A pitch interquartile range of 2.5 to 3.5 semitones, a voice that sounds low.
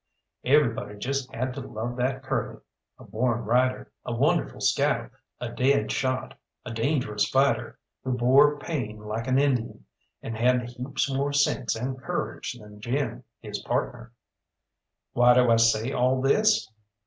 Yes: average, 2.8 semitones; low, 125 Hz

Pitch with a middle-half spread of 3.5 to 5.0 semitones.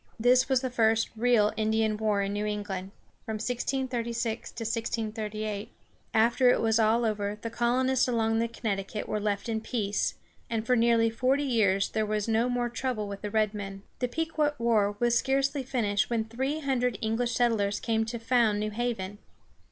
No: narrow, 2.5 semitones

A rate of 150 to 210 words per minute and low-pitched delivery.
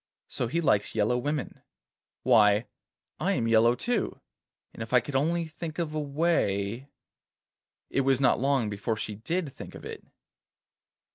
Yes: average, 155 wpm; low, 130 Hz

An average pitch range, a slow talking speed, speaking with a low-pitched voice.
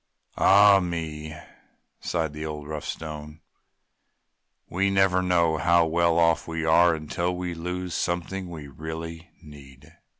No: narrow, 2.2 semitones; slow, 130 wpm; very low, 85 Hz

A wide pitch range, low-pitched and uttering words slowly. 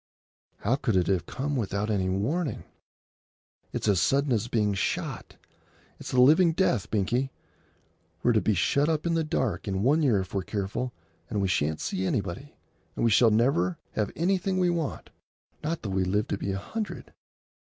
No: wide, 6.9 semitones; low, 110 Hz; average, 185 wpm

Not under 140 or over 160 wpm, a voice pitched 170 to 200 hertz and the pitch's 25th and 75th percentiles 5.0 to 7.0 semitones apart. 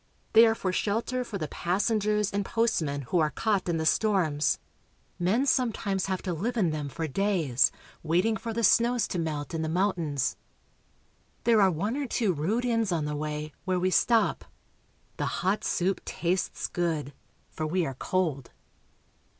No: average, 170 wpm; medium, 185 Hz; wide, 5.5 semitones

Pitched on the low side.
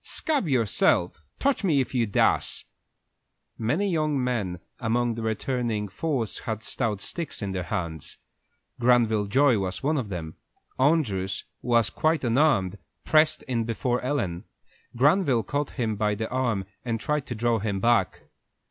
Yes: low, 120 Hz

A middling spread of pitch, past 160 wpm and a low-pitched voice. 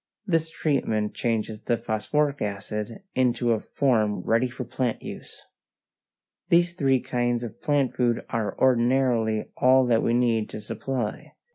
No: average, 3.0 semitones; average, 140 wpm; low, 120 Hz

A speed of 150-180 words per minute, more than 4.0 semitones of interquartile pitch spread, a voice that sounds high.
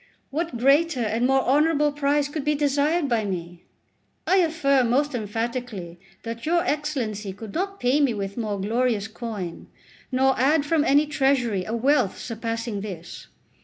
Yes: average, 155 wpm; average, 5.2 semitones; very high, 255 Hz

